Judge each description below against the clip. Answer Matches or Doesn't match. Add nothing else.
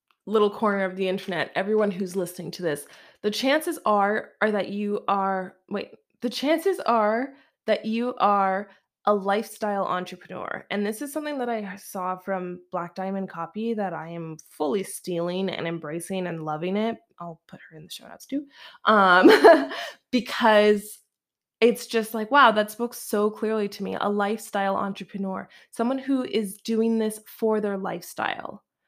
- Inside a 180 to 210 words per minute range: Doesn't match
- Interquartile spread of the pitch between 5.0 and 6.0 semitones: Doesn't match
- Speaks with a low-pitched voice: Doesn't match